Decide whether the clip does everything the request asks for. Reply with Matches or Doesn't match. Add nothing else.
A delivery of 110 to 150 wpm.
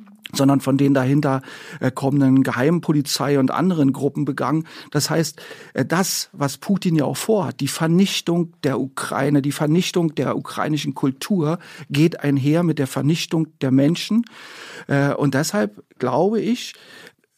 Matches